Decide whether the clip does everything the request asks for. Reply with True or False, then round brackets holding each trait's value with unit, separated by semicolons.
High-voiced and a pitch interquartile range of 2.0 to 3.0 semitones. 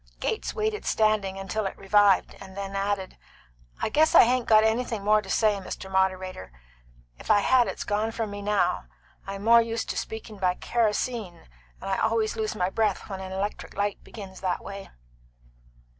True (205 Hz; 2.4 semitones)